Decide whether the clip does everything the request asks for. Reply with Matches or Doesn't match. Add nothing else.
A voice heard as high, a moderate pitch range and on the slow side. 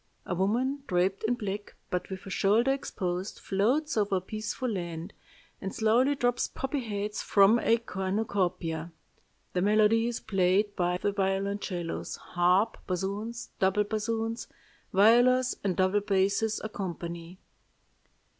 Matches